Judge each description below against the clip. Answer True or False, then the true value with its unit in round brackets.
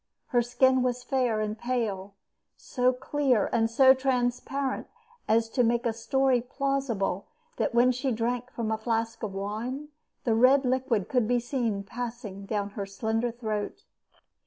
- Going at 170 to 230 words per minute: False (155 wpm)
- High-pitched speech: True (240 Hz)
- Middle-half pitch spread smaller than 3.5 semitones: True (2.6 semitones)